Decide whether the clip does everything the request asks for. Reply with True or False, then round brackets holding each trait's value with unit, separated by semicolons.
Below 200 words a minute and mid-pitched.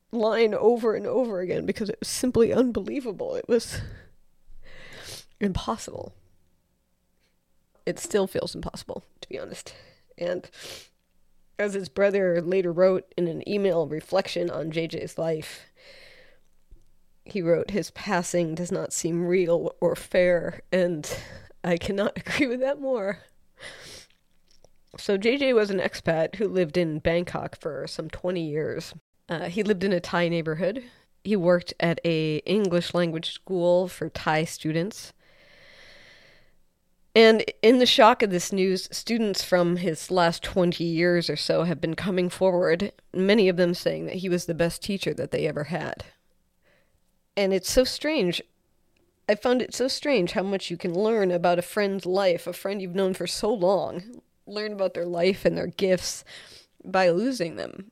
True (155 wpm; 180 Hz)